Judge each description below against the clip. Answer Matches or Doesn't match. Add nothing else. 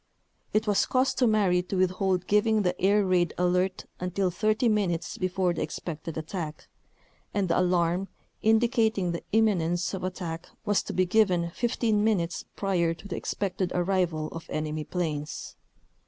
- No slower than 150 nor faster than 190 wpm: Matches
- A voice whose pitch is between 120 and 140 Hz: Doesn't match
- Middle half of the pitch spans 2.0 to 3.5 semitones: Matches